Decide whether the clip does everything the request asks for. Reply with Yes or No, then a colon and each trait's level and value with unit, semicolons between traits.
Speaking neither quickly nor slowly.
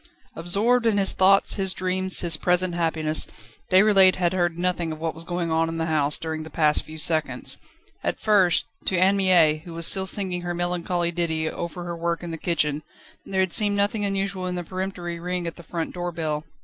No: fast, 210 wpm